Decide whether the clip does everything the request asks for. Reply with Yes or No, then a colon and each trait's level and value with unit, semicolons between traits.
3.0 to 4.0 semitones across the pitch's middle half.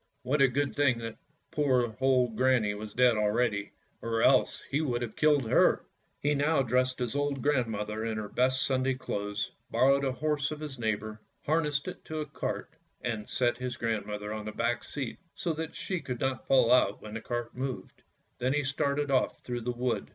Yes: average, 3.6 semitones